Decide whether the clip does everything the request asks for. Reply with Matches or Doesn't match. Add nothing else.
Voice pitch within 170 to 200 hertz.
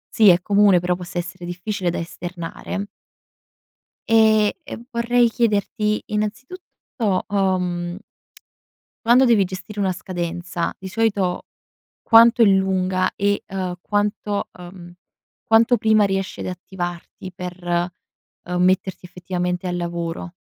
Matches